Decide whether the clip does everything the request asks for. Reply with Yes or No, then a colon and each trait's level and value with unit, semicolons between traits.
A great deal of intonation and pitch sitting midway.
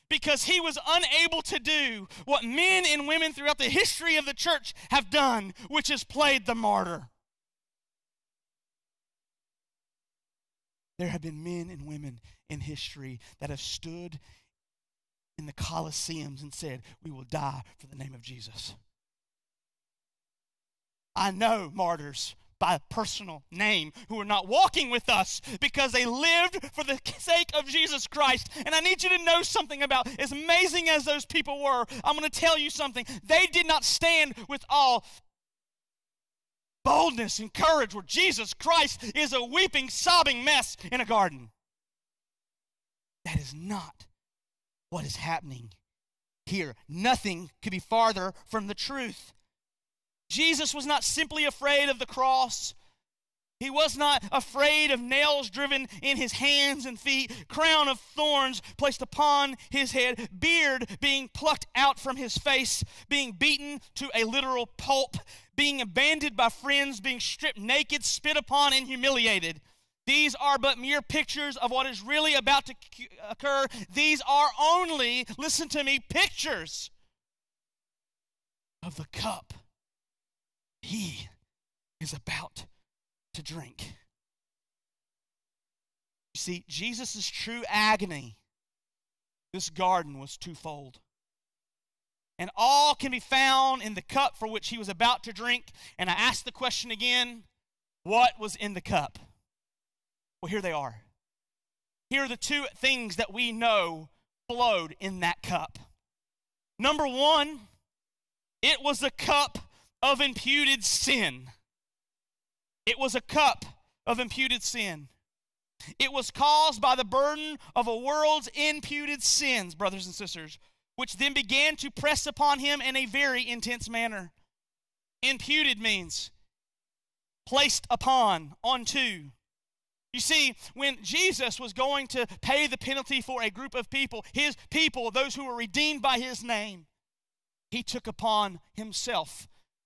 No: wide, 6.3 semitones; very high, 255 Hz